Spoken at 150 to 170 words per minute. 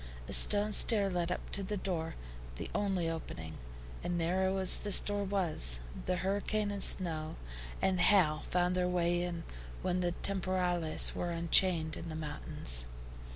Yes: average, 155 wpm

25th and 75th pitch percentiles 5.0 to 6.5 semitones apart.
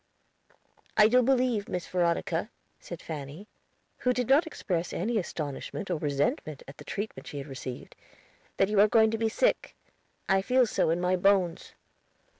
Yes: average, 5.3 semitones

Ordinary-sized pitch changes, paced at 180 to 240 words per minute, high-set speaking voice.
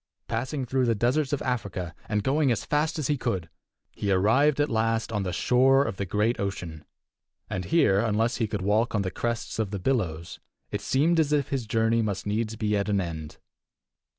No: average, 4.7 semitones; fast, 205 wpm; low, 115 Hz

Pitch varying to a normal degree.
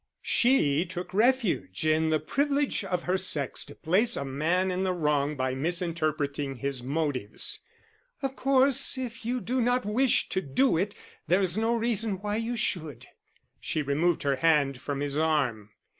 No: wide, 7.7 semitones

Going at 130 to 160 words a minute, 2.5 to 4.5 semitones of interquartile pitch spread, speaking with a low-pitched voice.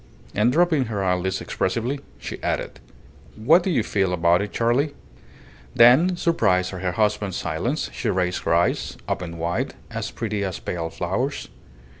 No: average, 155 wpm; average, 5.3 semitones; low, 100 Hz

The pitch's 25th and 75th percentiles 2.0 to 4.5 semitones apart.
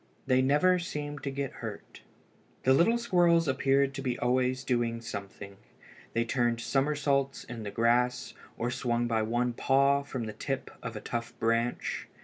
Yes: average, 2.9 semitones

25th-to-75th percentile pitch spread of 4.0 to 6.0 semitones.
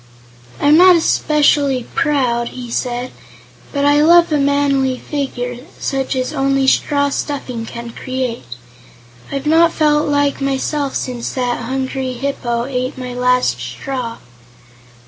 No: narrow, 2.6 semitones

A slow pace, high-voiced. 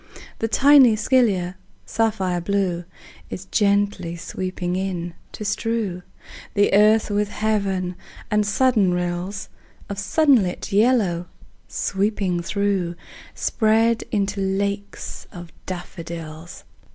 Yes: slow, 100 wpm; high, 200 Hz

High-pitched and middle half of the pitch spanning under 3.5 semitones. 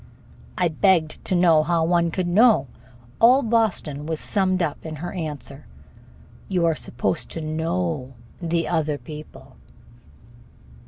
No: medium, 165 Hz; average, 3.0 semitones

